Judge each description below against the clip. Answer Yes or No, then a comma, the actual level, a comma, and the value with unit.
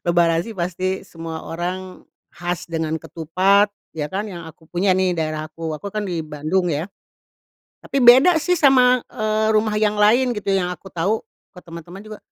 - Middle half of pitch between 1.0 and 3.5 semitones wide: No, average, 4.3 semitones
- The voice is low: No, medium, 185 Hz